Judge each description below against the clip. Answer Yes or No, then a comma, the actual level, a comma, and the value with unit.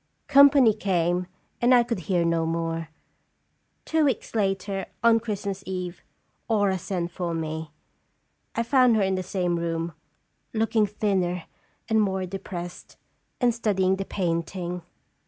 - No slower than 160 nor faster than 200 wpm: No, average, 140 wpm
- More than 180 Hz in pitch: Yes, high, 190 Hz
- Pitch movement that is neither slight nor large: Yes, average, 4.0 semitones